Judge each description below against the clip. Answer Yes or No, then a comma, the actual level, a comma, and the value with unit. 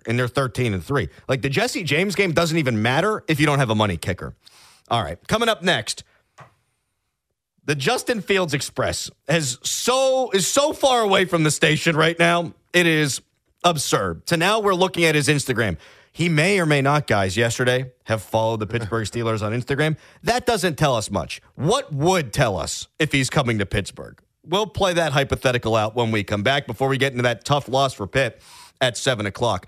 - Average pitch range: No, wide, 6.5 semitones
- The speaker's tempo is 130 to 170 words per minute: No, average, 200 wpm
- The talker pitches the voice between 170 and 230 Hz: No, medium, 140 Hz